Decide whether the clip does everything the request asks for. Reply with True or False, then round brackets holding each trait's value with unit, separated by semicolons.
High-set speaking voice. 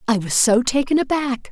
True (250 Hz)